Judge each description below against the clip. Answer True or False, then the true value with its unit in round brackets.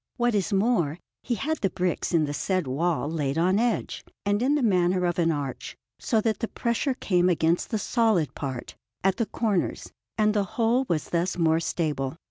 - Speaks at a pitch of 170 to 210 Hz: True (185 Hz)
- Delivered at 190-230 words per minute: True (195 wpm)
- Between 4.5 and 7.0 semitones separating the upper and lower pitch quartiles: True (5.4 semitones)